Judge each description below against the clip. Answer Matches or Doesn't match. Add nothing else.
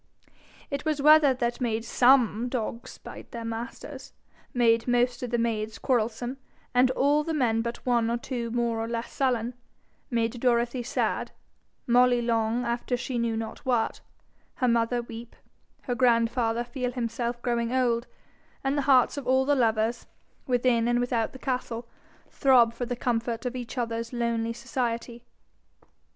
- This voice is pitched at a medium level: Doesn't match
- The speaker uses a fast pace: Doesn't match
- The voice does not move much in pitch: Matches